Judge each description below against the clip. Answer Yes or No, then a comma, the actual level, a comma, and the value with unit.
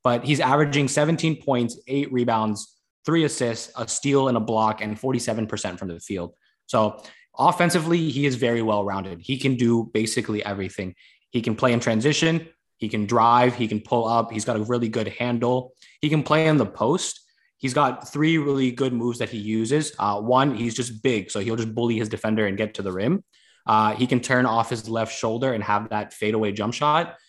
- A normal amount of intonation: Yes, average, 3.7 semitones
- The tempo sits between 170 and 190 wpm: No, fast, 205 wpm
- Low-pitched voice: Yes, low, 120 Hz